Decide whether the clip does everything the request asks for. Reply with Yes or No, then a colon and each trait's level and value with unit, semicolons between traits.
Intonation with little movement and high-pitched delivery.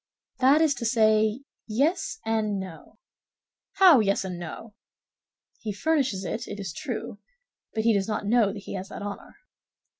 No: average, 3.4 semitones; high, 220 Hz